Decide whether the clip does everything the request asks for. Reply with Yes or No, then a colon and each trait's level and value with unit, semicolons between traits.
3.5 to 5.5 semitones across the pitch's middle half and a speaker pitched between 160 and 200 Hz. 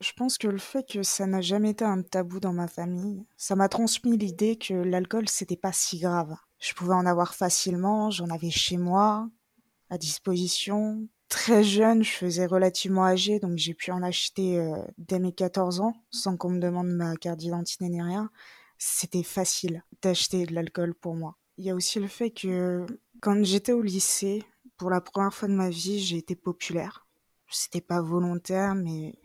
No: average, 2.7 semitones; medium, 185 Hz